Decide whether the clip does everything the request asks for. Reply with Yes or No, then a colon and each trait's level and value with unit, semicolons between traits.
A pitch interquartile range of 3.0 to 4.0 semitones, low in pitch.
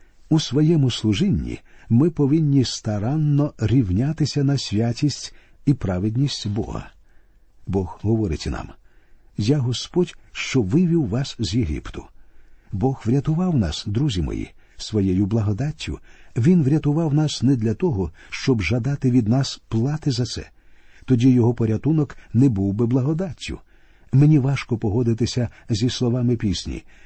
No: average, 4.9 semitones; low, 125 Hz